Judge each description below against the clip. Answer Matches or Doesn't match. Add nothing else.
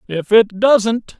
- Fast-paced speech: Doesn't match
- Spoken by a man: Matches